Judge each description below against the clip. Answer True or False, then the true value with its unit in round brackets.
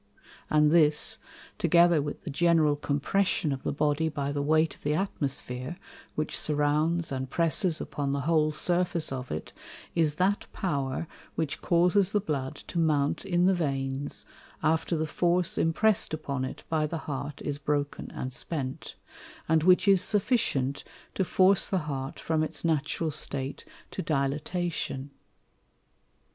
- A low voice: False (155 Hz)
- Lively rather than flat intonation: False (3.3 semitones)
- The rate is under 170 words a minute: True (150 wpm)